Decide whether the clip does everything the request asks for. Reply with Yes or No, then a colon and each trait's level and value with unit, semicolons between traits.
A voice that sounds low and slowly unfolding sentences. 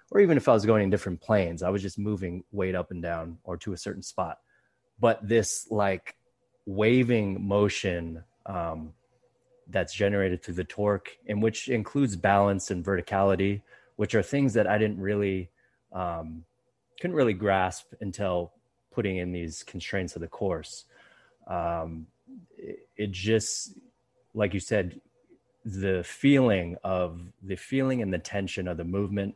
No: low, 100 Hz; average, 155 wpm